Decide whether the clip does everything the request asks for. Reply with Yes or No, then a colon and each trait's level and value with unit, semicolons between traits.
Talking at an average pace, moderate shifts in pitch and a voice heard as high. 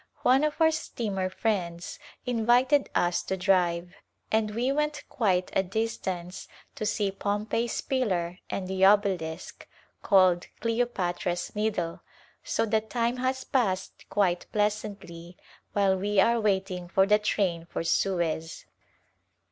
No: slow, 130 wpm; average, 4.0 semitones; high, 200 Hz